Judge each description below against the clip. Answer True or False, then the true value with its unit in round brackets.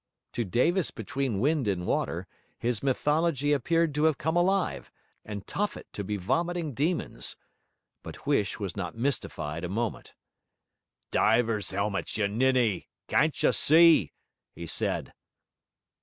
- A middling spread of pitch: False (7.5 semitones)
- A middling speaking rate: False (130 wpm)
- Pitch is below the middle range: True (130 Hz)